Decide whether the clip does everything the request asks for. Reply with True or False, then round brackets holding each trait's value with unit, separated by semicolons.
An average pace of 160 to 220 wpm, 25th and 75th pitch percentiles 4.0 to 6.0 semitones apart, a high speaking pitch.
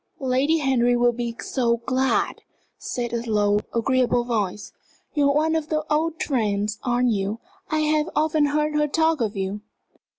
True (165 wpm; 4.7 semitones; 250 Hz)